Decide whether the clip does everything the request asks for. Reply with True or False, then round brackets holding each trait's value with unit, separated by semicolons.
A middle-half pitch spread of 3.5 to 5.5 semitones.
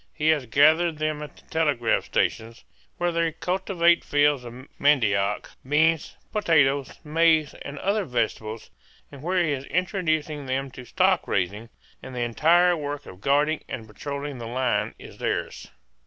True (4.4 semitones)